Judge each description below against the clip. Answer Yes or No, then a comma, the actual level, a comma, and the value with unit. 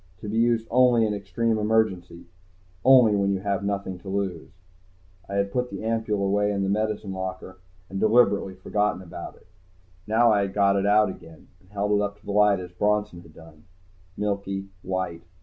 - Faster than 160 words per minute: Yes, average, 185 wpm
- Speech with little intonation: Yes, narrow, 1.9 semitones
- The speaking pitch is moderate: No, low, 100 Hz